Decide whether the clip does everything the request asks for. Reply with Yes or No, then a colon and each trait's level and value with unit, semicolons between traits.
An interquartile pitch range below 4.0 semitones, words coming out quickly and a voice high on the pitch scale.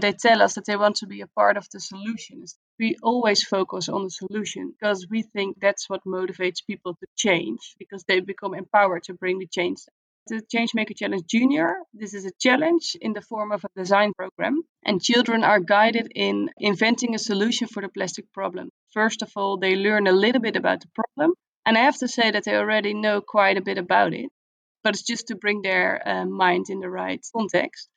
Yes: average, 2.9 semitones; fast, 215 wpm; high, 205 Hz